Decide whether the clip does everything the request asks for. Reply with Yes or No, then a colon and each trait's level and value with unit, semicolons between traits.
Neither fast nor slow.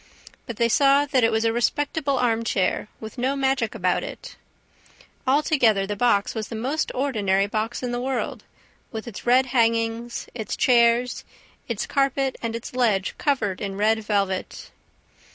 Yes: average, 160 wpm